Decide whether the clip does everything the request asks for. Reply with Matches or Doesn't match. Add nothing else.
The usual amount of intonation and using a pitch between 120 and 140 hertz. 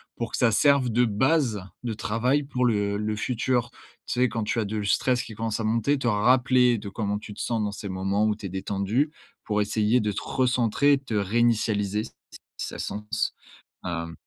Doesn't match